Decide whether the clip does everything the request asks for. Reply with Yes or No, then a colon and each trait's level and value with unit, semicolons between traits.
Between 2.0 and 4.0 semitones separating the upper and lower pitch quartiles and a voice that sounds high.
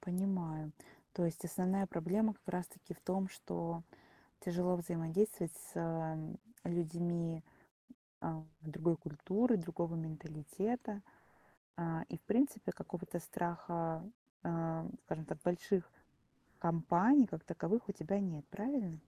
No: average, 2.9 semitones; medium, 170 Hz